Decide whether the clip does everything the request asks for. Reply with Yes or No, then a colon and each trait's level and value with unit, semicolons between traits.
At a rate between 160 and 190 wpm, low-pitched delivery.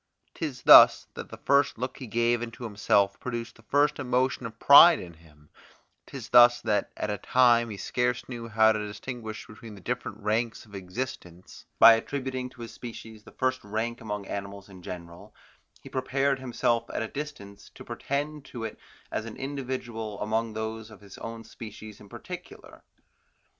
Yes: average, 175 wpm; low, 115 Hz